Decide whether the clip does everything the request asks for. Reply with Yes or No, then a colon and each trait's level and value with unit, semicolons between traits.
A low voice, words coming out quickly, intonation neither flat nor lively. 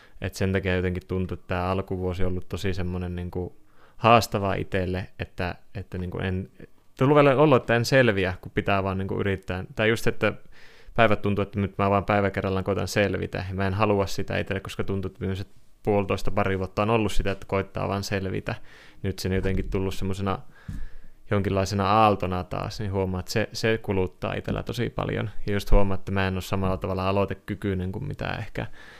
No: low, 100 Hz; fast, 195 wpm; narrow, 2.0 semitones